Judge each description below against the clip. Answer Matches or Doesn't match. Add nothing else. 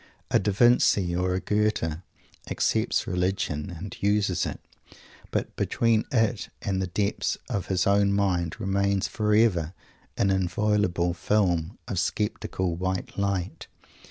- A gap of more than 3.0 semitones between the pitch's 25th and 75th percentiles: Doesn't match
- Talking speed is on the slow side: Matches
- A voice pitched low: Matches